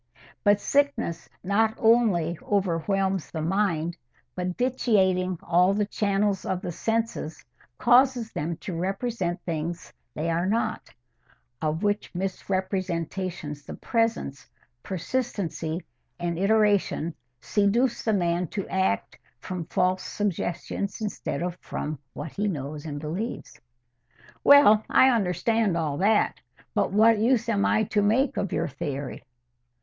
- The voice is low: No, high, 190 Hz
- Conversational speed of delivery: No, slow, 125 wpm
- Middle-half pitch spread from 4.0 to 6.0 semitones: Yes, average, 4.4 semitones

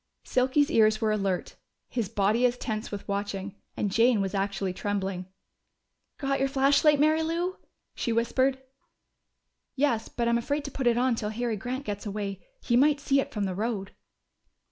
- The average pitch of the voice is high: Yes, high, 230 Hz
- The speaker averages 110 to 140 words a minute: No, average, 170 wpm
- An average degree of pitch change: Yes, average, 4.9 semitones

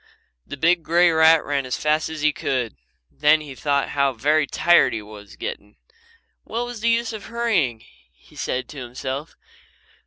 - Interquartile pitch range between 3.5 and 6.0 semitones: Yes, average, 4.6 semitones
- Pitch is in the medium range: Yes, medium, 150 Hz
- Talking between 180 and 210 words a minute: No, average, 165 wpm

